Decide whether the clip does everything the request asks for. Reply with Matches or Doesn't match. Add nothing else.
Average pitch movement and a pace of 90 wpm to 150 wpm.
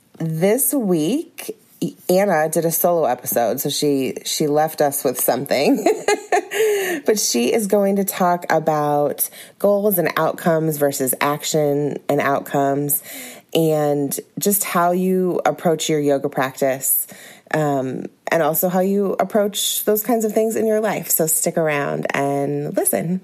Doesn't match